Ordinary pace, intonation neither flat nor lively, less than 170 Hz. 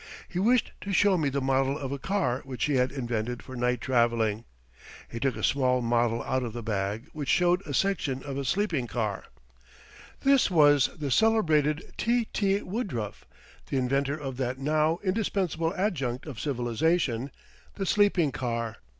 No: average, 165 wpm; wide, 6.2 semitones; low, 135 Hz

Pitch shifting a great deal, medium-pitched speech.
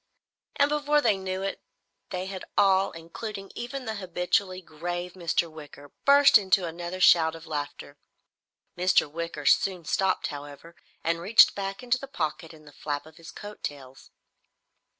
No: average, 3.6 semitones; medium, 180 Hz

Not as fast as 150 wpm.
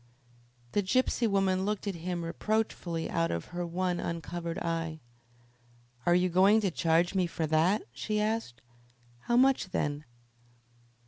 Yes: average, 140 wpm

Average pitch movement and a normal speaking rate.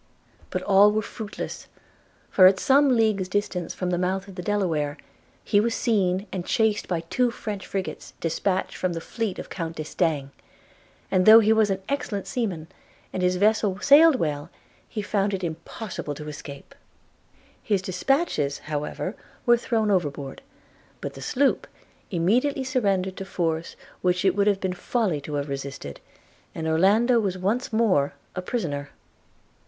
Yes: average, 4.8 semitones; average, 160 wpm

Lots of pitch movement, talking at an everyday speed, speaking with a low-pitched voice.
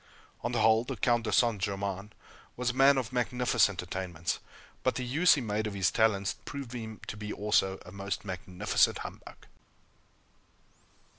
No: average, 3.9 semitones; average, 165 wpm; low, 110 Hz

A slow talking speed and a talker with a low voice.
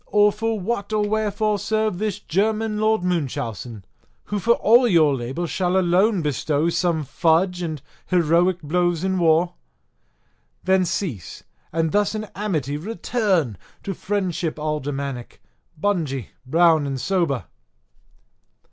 No: slow, 125 wpm; medium, 175 Hz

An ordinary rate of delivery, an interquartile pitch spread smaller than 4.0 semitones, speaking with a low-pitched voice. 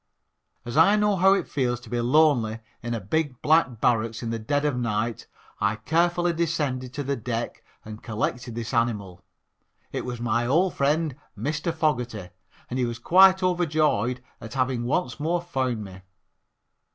No: average, 165 wpm; wide, 5.4 semitones; low, 125 Hz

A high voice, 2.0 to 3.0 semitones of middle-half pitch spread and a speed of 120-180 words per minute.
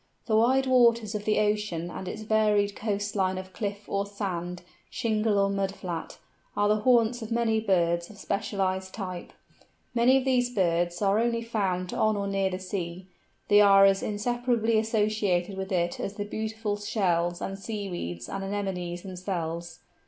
Yes: high, 200 Hz; average, 2.7 semitones; average, 165 wpm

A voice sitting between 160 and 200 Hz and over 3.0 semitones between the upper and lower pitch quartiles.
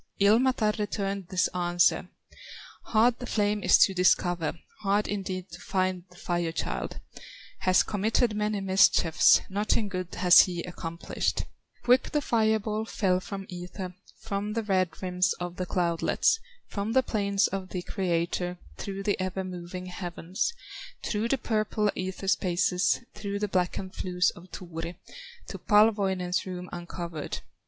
No: high, 190 Hz; narrow, 2.6 semitones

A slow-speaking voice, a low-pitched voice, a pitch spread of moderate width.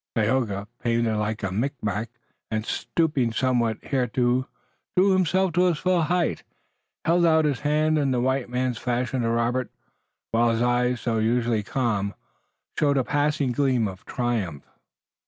No: average, 150 wpm; low, 125 Hz; average, 4.1 semitones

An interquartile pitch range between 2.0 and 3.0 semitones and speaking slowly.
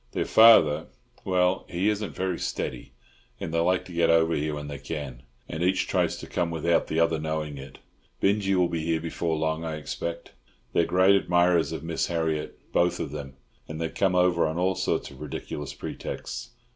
No: narrow, 2.4 semitones; average, 190 wpm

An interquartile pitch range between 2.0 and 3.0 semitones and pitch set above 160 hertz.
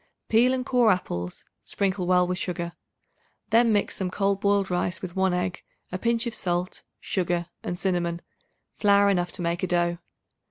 Yes: narrow, 2.4 semitones; medium, 185 Hz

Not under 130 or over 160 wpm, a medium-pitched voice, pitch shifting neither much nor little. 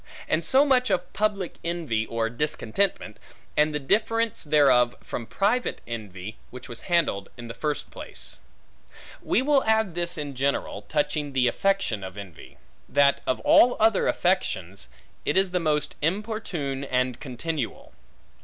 No: average, 145 wpm; medium, 150 Hz; wide, 8.3 semitones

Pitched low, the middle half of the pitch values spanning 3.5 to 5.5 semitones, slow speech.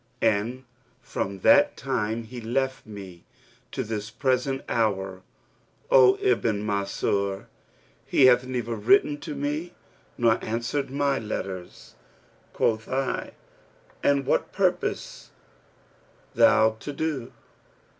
Yes: low, 120 Hz; average, 4.6 semitones; slow, 105 wpm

